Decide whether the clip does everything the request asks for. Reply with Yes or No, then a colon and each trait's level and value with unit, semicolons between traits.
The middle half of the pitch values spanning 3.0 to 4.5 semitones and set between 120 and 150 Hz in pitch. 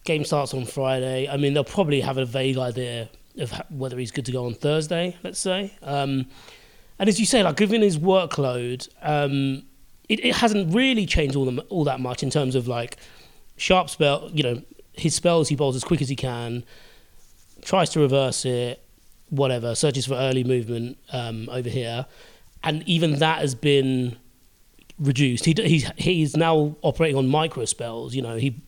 Yes: average, 4.1 semitones; medium, 140 Hz